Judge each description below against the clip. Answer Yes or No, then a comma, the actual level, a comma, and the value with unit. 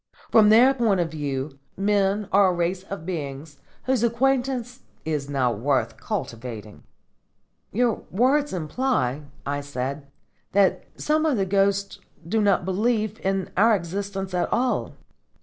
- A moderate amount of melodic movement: No, wide, 7.2 semitones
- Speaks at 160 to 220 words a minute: No, slow, 135 wpm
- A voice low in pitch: No, high, 195 Hz